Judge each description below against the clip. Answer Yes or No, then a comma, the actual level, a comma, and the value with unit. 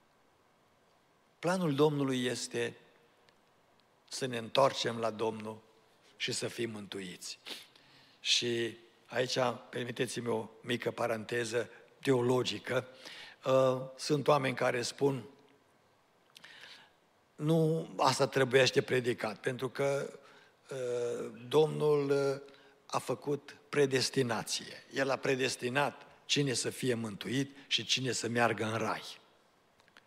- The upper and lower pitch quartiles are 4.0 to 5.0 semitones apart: No, average, 2.9 semitones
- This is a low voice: Yes, low, 125 Hz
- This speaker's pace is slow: Yes, slow, 90 wpm